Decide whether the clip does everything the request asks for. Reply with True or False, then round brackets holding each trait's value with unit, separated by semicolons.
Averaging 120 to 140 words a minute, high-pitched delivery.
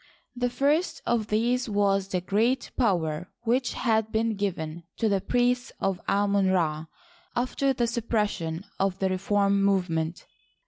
True (135 wpm; 205 Hz)